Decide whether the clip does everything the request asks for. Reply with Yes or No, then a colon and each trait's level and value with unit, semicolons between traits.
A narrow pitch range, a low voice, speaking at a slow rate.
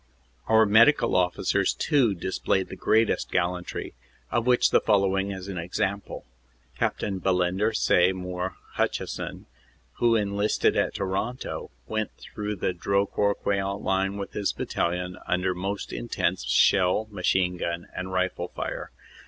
Yes: narrow, 2.2 semitones; very low, 95 Hz; slow, 130 wpm